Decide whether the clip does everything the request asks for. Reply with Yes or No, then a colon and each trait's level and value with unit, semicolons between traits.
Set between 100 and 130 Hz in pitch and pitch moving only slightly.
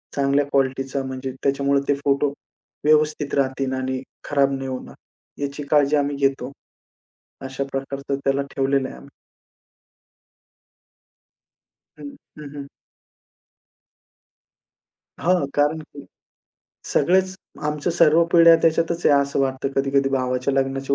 No: medium, 140 Hz; narrow, 1.5 semitones